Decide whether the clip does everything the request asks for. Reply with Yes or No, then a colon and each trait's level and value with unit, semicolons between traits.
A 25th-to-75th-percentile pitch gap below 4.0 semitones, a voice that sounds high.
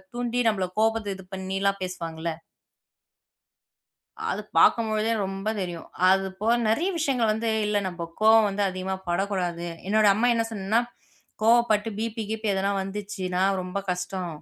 Yes: average, 3.0 semitones; high, 200 Hz